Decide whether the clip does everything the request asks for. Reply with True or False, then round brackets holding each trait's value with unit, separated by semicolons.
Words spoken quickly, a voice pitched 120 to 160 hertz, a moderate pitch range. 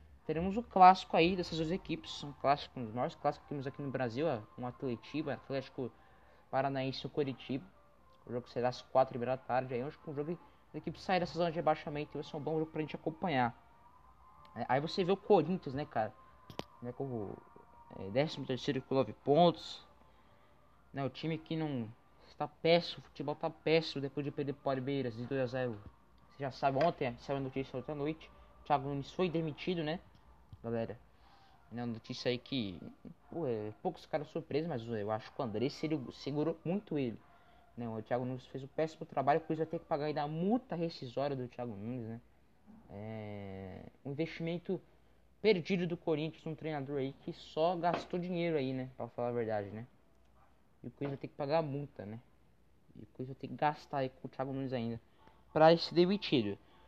True (200 wpm; 140 Hz; 4.4 semitones)